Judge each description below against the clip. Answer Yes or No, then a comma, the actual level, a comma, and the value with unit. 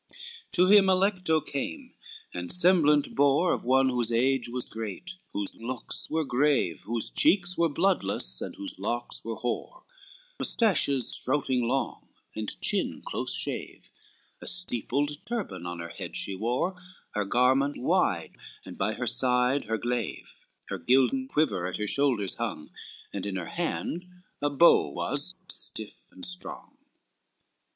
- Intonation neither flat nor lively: No, wide, 6.7 semitones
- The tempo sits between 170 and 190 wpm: No, average, 145 wpm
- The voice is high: No, low, 130 Hz